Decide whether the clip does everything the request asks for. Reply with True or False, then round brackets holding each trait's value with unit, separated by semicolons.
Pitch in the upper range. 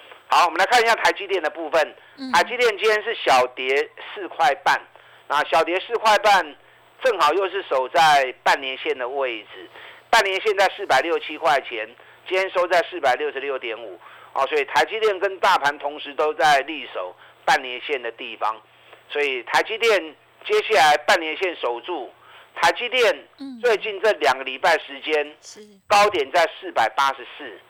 True (220 Hz)